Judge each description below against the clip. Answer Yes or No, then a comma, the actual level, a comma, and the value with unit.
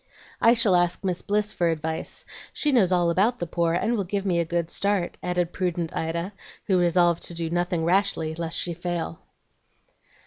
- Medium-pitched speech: Yes, medium, 175 Hz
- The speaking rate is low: No, average, 195 wpm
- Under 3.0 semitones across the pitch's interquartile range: Yes, narrow, 2.4 semitones